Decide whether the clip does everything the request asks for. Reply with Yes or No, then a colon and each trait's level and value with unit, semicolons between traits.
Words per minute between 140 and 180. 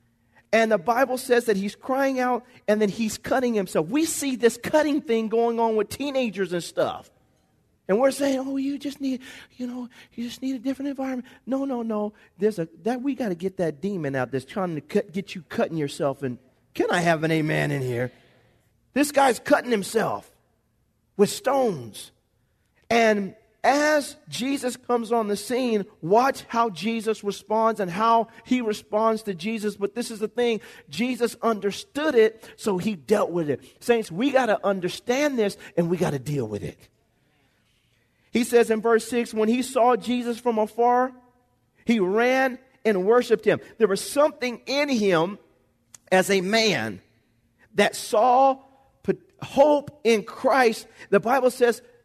Yes: average, 170 wpm